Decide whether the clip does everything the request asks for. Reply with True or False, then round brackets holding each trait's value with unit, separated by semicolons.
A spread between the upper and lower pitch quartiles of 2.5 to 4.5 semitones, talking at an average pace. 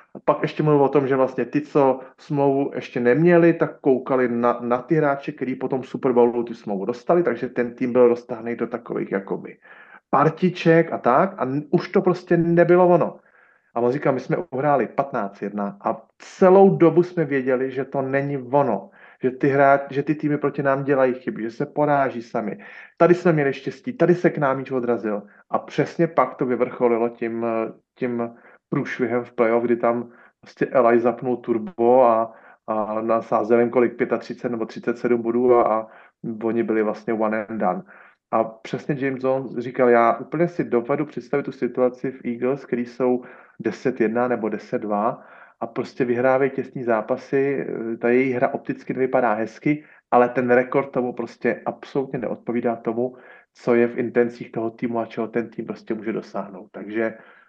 False (2.9 semitones; 170 wpm)